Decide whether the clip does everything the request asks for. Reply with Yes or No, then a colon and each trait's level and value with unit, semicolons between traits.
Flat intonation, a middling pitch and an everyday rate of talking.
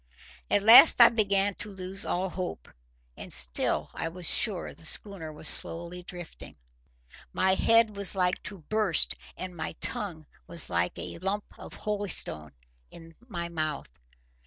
No: average, 3.6 semitones; medium, 180 Hz; average, 150 wpm